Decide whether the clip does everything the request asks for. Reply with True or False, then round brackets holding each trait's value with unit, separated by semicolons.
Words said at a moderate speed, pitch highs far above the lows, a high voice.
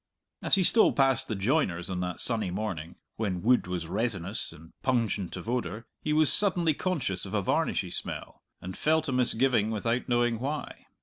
False (180 wpm; 6.2 semitones; 115 Hz)